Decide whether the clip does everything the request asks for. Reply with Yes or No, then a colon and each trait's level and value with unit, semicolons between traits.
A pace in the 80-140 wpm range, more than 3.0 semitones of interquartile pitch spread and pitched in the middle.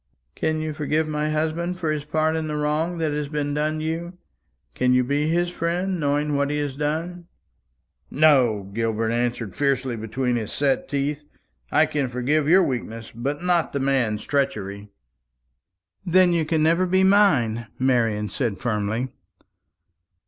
No: average, 155 wpm; average, 4.4 semitones; medium, 145 Hz